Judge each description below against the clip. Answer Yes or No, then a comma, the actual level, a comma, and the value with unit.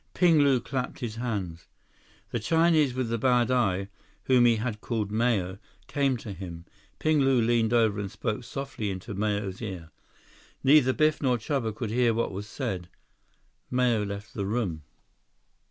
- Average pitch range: Yes, average, 3.9 semitones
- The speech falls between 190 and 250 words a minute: No, average, 160 wpm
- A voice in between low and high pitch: No, low, 115 Hz